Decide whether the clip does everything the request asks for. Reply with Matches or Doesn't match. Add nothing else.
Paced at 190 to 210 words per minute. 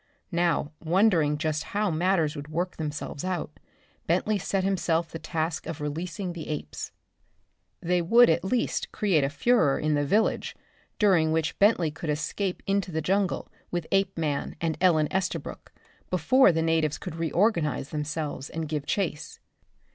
Doesn't match